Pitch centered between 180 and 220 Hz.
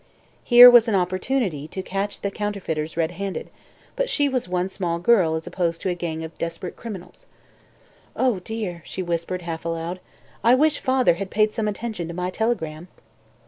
Yes: medium, 185 Hz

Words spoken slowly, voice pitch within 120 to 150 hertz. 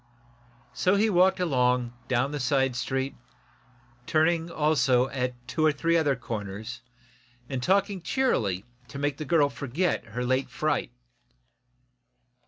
Yes: slow, 125 wpm; medium, 140 Hz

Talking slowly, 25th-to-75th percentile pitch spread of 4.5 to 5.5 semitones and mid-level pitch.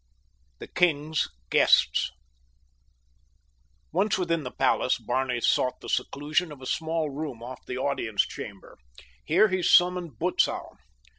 Yes: slow, 125 wpm; average, 5.1 semitones; medium, 150 Hz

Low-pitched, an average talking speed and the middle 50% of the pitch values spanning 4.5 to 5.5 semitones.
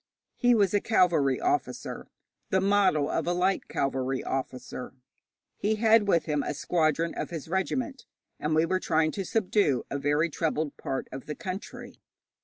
No: medium, 170 Hz; average, 165 wpm; average, 5.2 semitones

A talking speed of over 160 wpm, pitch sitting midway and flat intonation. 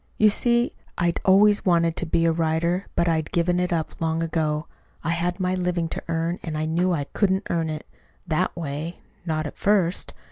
Yes: average, 200 wpm; medium, 170 Hz; narrow, 2.0 semitones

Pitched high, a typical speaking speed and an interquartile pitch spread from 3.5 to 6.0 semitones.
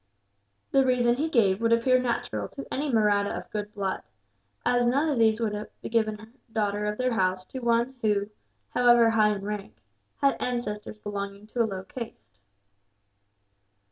No: high, 220 Hz; average, 170 wpm; average, 2.8 semitones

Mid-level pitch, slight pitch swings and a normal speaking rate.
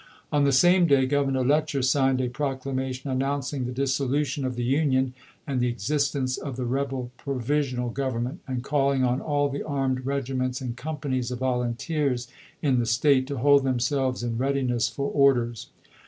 No: low, 130 Hz; narrow, 2.0 semitones; average, 170 wpm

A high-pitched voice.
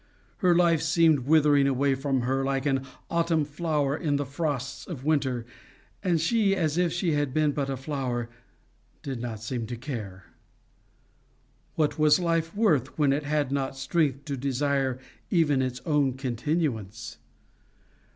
No: medium, 140 Hz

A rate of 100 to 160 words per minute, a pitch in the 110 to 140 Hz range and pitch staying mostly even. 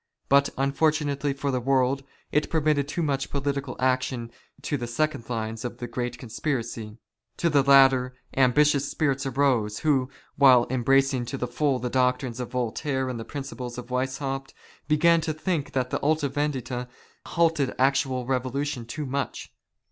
Yes: average, 155 wpm; low, 135 Hz; narrow, 2.3 semitones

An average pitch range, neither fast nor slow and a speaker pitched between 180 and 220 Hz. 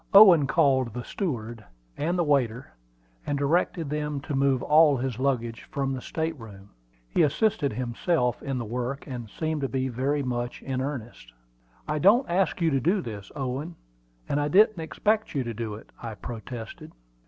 No: average, 4.5 semitones; average, 175 wpm; low, 135 Hz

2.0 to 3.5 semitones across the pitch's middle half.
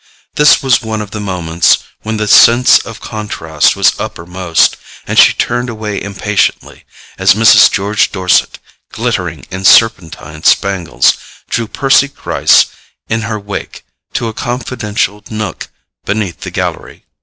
Yes: average, 3.2 semitones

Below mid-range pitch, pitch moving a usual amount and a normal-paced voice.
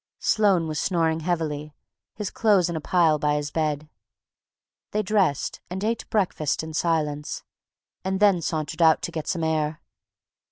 No: medium, 160 Hz; average, 3.7 semitones; average, 155 wpm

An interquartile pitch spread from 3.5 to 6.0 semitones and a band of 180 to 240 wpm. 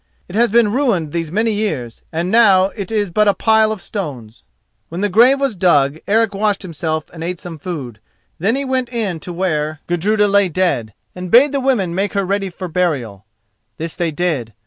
Yes: average, 5.0 semitones; average, 200 wpm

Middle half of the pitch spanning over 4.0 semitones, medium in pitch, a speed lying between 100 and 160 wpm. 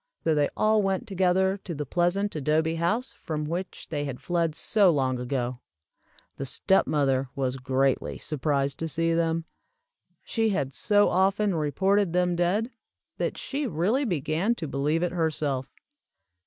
Yes: average, 5.0 semitones; medium, 165 Hz; average, 155 wpm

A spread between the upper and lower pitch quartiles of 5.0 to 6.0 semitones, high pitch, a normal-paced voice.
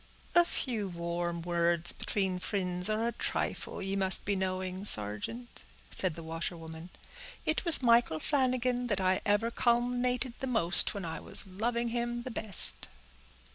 Yes: wide, 5.4 semitones; high, 200 Hz; average, 150 wpm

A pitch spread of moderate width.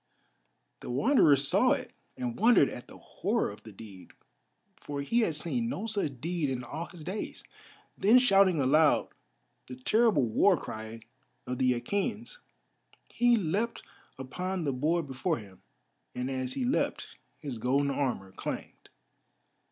No: wide, 7.8 semitones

